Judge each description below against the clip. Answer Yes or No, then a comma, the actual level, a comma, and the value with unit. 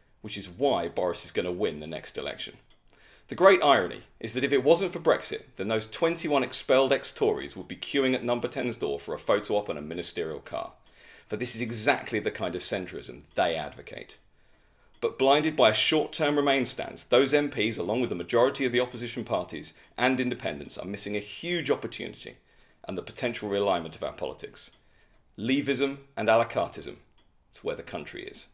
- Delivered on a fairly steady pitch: No, average, 3.8 semitones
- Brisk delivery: No, average, 195 wpm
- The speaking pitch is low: Yes, low, 130 Hz